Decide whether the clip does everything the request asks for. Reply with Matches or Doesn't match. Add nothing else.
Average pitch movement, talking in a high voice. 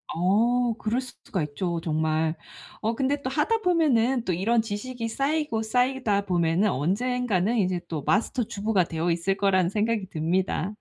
Doesn't match